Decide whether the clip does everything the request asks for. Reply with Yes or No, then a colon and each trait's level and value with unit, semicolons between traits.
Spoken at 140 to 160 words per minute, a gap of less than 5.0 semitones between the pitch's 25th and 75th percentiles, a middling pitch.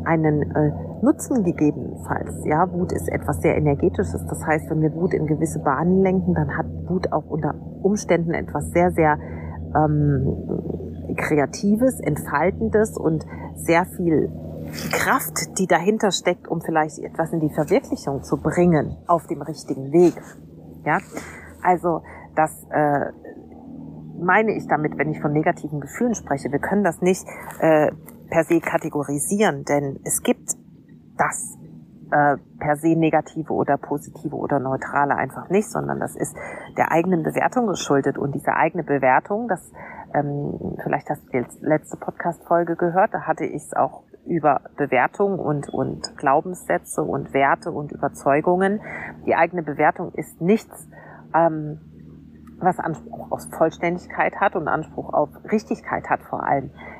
Yes: average, 145 wpm; average, 3.5 semitones; medium, 160 Hz